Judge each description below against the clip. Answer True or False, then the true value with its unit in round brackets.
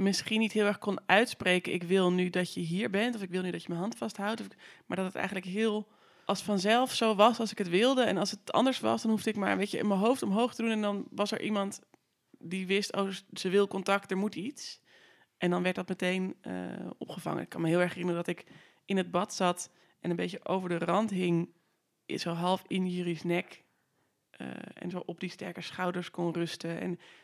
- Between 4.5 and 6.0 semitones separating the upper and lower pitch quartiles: False (2.9 semitones)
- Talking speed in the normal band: False (240 wpm)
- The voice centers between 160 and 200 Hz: True (190 Hz)